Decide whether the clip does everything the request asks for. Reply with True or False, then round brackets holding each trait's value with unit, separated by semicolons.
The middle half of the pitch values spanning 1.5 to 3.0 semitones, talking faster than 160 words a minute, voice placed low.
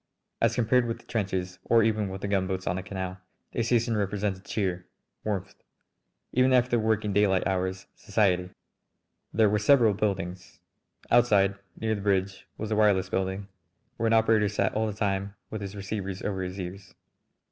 True (2.5 semitones; 170 wpm; 100 Hz)